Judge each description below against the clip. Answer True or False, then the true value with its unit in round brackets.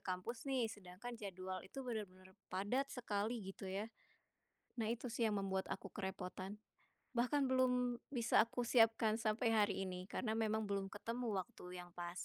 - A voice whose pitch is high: True (215 Hz)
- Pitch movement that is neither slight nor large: True (4.0 semitones)